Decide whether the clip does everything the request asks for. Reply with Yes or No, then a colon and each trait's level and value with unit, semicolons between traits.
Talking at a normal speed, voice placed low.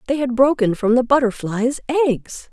No: average, 165 wpm; very high, 250 Hz